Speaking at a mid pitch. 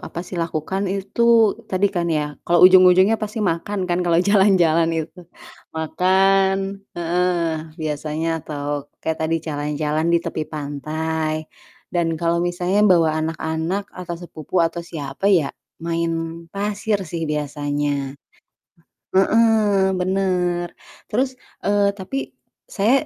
Yes: medium, 175 Hz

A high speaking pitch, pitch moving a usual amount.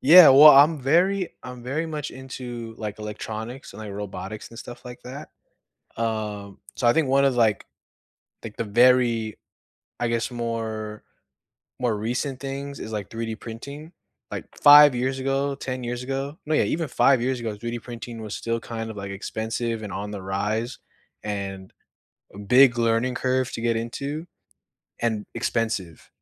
No: low, 120 Hz; average, 3.5 semitones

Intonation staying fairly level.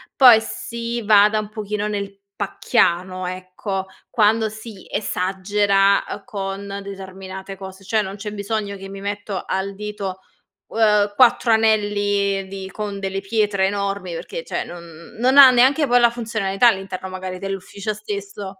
Yes: narrow, 1.9 semitones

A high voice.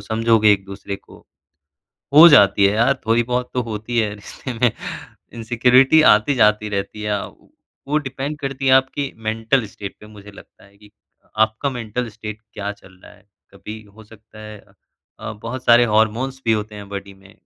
No: low, 110 Hz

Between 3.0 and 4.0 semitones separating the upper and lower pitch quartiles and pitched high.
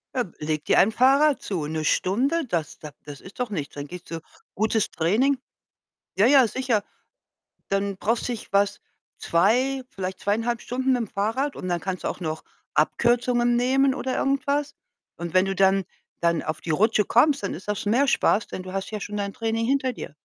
No: wide, 5.5 semitones; high, 210 Hz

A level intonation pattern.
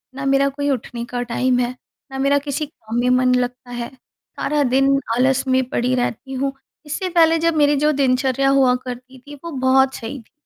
Yes: narrow, 2.1 semitones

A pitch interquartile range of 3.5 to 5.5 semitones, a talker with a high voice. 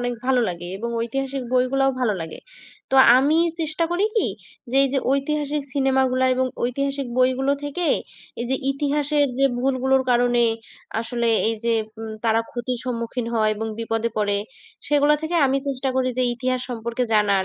No: average, 2.9 semitones; very high, 255 Hz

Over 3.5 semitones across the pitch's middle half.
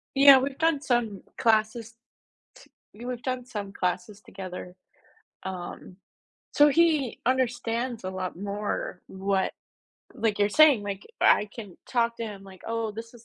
Yes: average, 4.1 semitones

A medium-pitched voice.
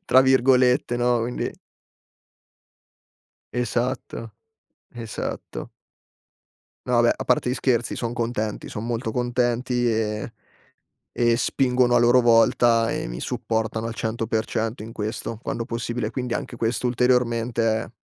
No: low, 120 Hz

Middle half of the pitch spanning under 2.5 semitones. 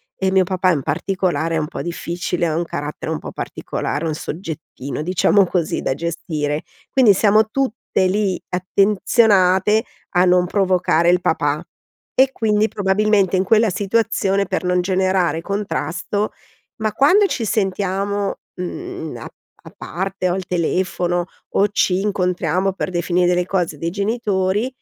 No: average, 2.8 semitones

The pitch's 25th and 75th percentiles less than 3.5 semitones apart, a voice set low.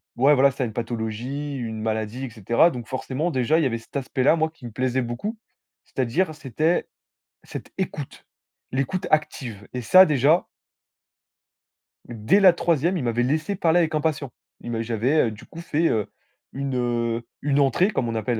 No: average, 4.9 semitones; low, 130 Hz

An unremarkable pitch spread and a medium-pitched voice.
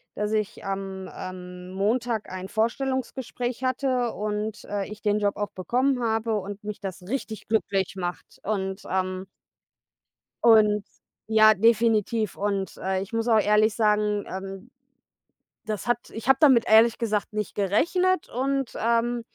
No: average, 3.0 semitones; high, 215 Hz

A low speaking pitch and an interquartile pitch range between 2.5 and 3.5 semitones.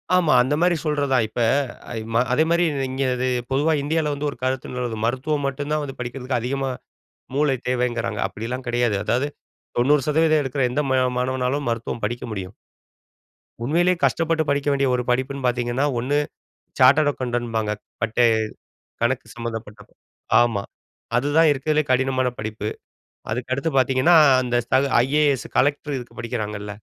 Yes: low, 130 Hz; average, 3.1 semitones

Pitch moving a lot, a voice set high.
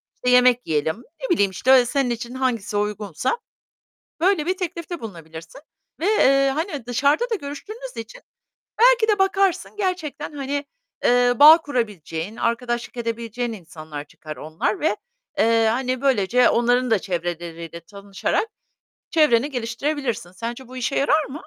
Yes: wide, 6.3 semitones; high, 245 Hz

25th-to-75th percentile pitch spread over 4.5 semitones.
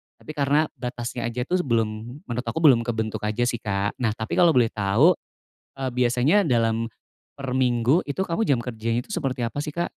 No: average, 3.8 semitones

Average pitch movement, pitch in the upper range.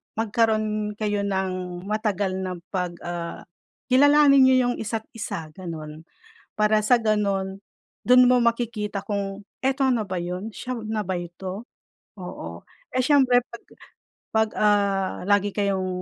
Yes: average, 3.2 semitones; high, 205 Hz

